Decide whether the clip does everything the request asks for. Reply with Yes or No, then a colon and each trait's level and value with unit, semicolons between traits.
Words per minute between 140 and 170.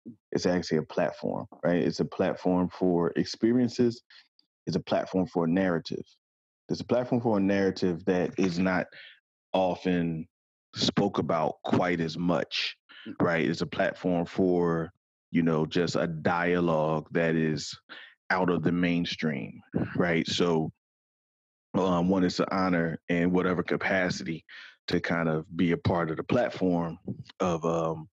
Yes: average, 145 wpm